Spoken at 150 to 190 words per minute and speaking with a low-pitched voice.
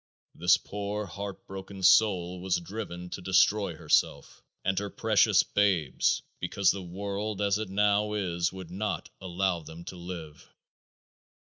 No: average, 140 wpm; very low, 95 Hz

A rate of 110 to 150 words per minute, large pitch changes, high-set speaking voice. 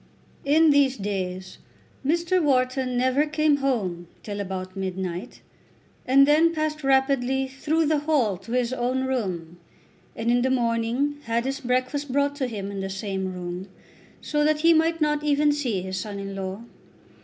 No: average, 165 wpm; wide, 6.7 semitones; very high, 255 Hz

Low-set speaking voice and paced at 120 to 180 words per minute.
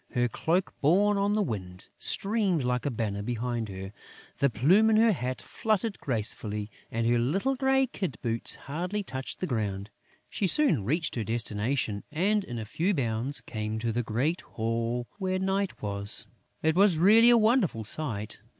Yes: low, 130 Hz; average, 170 wpm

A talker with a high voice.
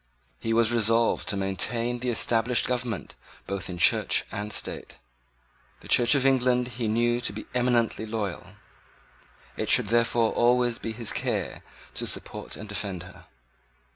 No: low, 115 Hz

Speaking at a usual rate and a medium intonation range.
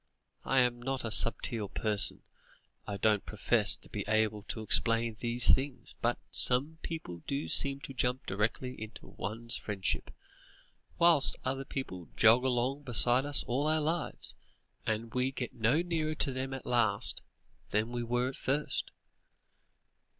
Yes: average, 150 wpm; average, 3.5 semitones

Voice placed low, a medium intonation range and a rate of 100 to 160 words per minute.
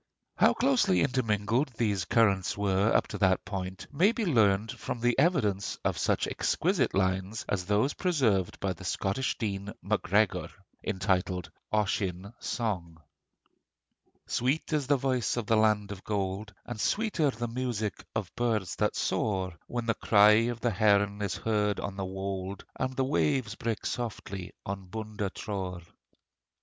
Yes: low, 105 Hz; average, 3.8 semitones; average, 150 wpm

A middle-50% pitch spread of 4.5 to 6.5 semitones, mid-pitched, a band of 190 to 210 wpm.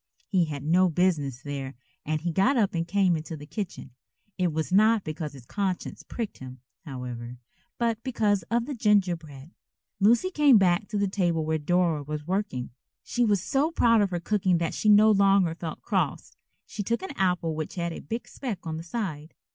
Yes: average, 5.0 semitones; medium, 180 Hz; average, 195 wpm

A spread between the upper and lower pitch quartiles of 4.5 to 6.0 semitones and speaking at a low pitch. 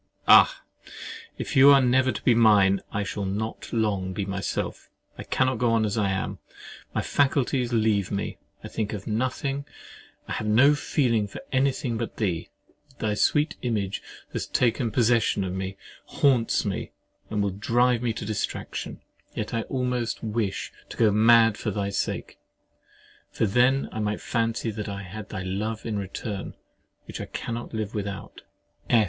No: average, 3.2 semitones; low, 110 Hz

